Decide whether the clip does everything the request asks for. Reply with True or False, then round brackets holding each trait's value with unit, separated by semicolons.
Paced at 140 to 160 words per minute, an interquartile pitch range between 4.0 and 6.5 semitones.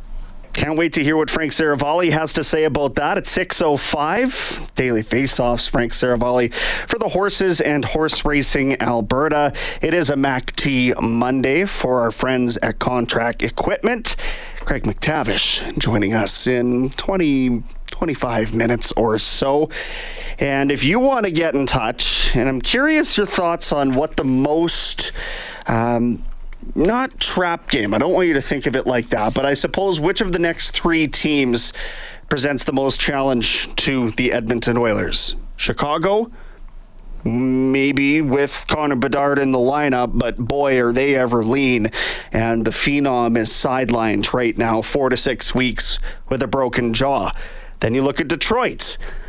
True (155 wpm; 4.3 semitones)